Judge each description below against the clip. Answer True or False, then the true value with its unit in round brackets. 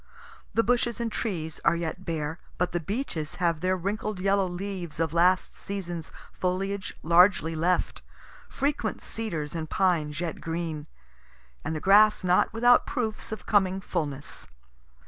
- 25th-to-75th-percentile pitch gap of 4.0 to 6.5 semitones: False (3.5 semitones)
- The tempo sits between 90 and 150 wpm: True (145 wpm)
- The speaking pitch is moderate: True (180 Hz)